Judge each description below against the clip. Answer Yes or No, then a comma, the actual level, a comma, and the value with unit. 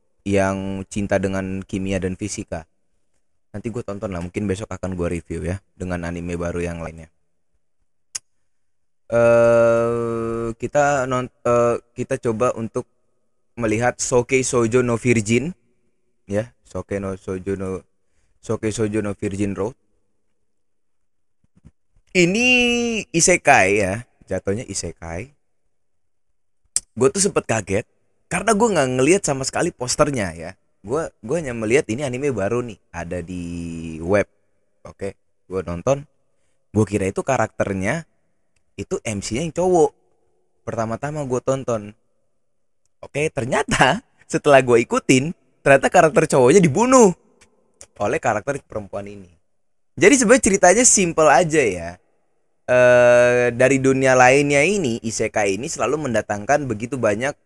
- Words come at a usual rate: Yes, average, 120 wpm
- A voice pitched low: Yes, low, 110 Hz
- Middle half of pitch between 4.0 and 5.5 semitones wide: Yes, average, 5.1 semitones